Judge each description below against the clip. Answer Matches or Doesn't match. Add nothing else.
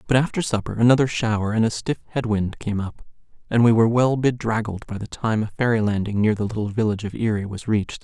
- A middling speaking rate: Doesn't match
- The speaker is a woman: Doesn't match